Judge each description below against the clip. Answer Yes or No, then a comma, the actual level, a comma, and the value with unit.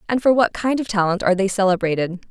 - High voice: Yes, high, 205 Hz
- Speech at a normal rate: No, fast, 235 wpm